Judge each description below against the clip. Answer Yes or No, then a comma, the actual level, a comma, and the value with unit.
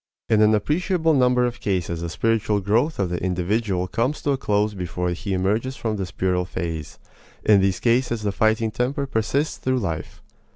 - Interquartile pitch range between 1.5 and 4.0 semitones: No, average, 5.0 semitones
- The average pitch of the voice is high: No, low, 105 Hz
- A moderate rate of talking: Yes, average, 180 wpm